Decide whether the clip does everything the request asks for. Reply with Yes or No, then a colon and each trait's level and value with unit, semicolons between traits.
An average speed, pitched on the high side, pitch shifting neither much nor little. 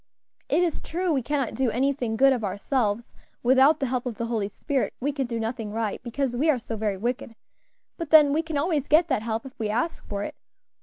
No: fast, 225 wpm; very high, 255 Hz; average, 4.3 semitones